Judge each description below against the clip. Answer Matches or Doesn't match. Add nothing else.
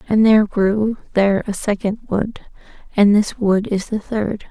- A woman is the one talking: Matches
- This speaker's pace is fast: Doesn't match